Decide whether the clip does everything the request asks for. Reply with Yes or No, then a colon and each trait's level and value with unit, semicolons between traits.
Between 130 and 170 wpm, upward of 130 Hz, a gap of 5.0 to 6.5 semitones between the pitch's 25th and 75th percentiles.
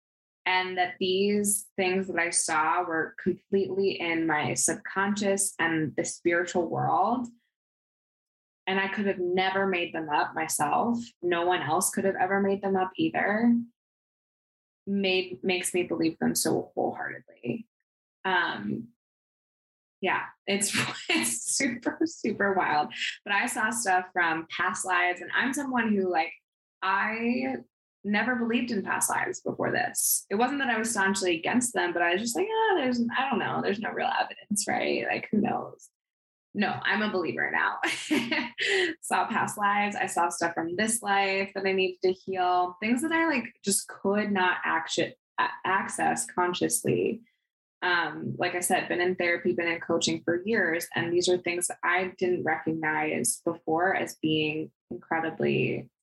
No: average, 155 wpm; high, 190 Hz; average, 4.0 semitones